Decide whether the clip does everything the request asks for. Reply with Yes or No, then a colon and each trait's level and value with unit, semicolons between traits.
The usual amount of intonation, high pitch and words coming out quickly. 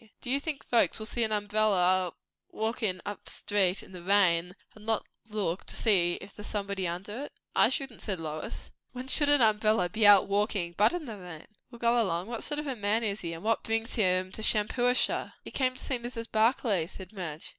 Yes: average, 4.0 semitones; high, 210 Hz; fast, 215 wpm